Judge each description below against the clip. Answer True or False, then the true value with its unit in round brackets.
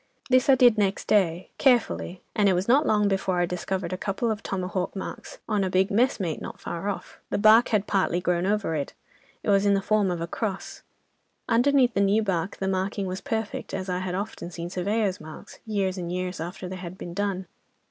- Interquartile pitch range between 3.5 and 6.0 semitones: False (2.6 semitones)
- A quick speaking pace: True (220 wpm)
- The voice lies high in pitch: True (195 Hz)